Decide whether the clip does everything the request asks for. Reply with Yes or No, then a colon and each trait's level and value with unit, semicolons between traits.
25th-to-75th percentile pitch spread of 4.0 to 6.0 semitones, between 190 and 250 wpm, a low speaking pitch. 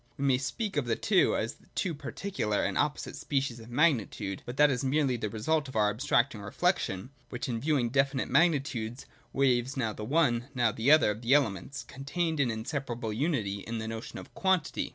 Yes: average, 4.4 semitones; average, 195 wpm; low, 130 Hz